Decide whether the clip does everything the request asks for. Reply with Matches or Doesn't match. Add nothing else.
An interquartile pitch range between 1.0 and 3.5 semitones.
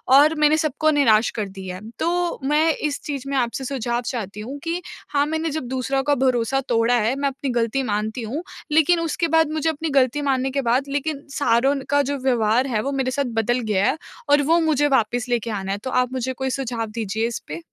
Doesn't match